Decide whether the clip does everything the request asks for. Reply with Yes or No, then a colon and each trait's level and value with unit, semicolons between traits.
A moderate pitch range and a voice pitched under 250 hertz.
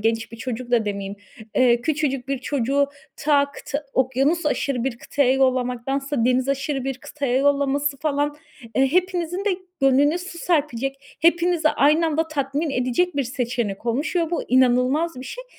No: average, 3.1 semitones; very high, 275 Hz